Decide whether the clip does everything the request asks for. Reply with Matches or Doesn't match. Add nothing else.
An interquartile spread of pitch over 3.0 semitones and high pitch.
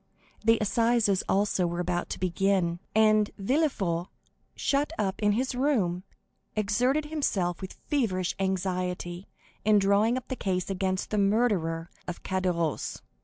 Matches